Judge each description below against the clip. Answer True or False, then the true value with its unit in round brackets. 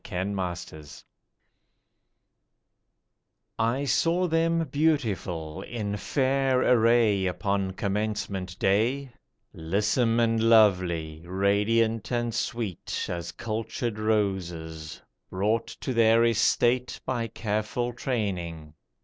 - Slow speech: True (90 wpm)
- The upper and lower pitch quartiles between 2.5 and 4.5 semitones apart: True (4.2 semitones)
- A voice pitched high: False (110 Hz)